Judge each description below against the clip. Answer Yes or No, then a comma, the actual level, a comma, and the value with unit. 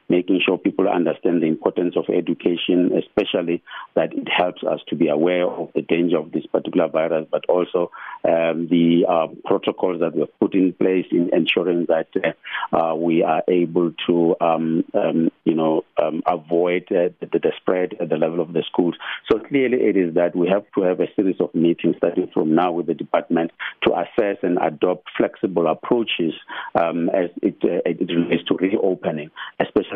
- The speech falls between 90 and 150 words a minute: No, average, 190 wpm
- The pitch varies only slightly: Yes, narrow, 1.3 semitones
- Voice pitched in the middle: No, very low, 85 Hz